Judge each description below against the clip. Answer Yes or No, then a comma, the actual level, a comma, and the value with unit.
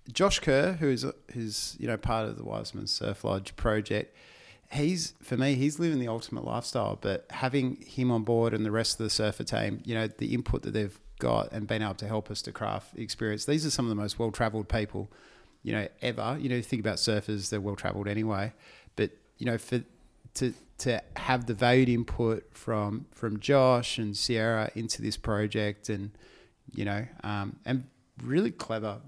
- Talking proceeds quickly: No, average, 195 wpm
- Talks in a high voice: No, low, 110 Hz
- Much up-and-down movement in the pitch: No, average, 2.9 semitones